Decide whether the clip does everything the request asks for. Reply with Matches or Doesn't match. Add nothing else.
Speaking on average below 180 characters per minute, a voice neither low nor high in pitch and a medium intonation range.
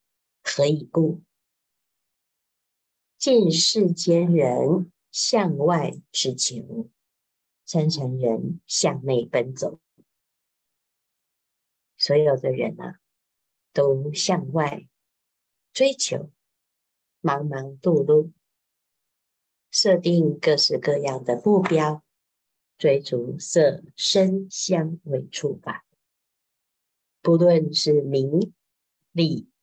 Matches